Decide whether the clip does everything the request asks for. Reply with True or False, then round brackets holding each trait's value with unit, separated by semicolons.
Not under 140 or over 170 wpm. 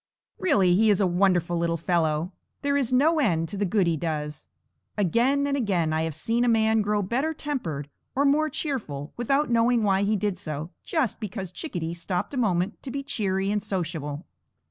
False (190 wpm)